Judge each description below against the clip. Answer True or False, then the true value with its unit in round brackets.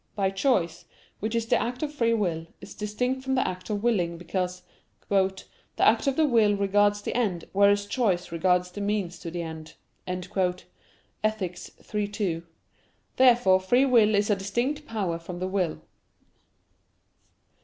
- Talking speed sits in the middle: True (155 wpm)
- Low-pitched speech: False (200 Hz)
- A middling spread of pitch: True (3.9 semitones)